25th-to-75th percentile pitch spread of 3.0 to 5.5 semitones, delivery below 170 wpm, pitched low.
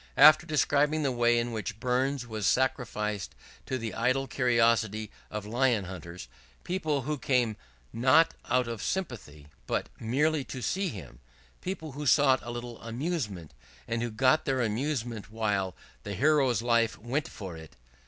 Yes: average, 4.2 semitones; average, 155 wpm; low, 120 Hz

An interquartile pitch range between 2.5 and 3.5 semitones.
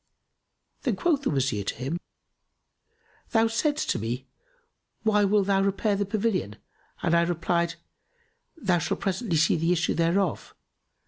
No: average, 4.1 semitones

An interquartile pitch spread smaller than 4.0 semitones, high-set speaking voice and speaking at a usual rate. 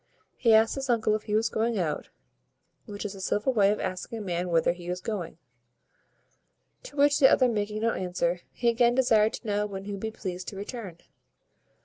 No: average, 3.6 semitones; high, 210 Hz; fast, 210 wpm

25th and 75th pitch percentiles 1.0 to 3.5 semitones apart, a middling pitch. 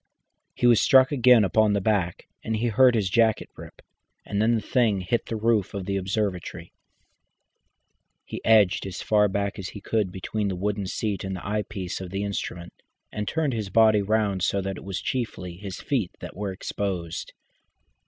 No: narrow, 2.6 semitones; low, 100 Hz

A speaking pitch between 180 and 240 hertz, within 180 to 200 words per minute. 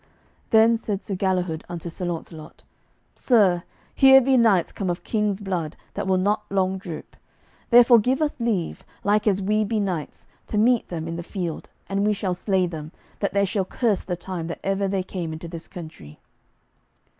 Yes: high, 190 Hz; average, 185 wpm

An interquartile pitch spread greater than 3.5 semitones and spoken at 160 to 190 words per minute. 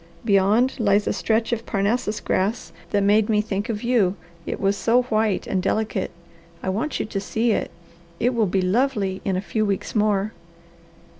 No: narrow, 2.5 semitones; average, 180 wpm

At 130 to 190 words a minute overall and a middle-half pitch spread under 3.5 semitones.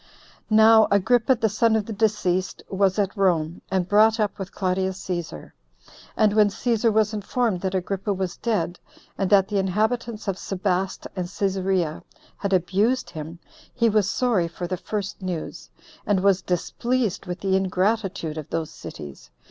Yes: average, 165 wpm; average, 3.0 semitones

